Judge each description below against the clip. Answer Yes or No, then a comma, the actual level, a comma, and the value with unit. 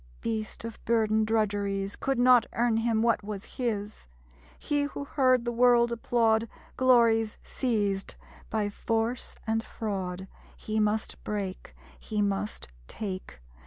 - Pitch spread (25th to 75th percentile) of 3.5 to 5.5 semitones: No, narrow, 2.4 semitones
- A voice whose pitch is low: No, high, 220 Hz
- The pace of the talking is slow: Yes, slow, 125 wpm